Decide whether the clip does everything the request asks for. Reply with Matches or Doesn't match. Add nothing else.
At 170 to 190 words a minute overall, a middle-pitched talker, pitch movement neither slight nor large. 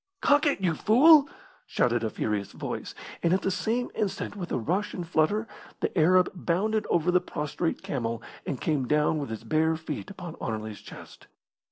Doesn't match